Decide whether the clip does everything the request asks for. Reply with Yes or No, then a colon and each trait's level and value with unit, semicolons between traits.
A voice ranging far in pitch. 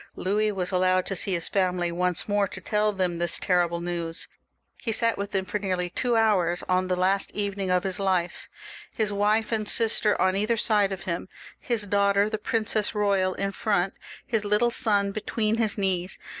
No: narrow, 2.5 semitones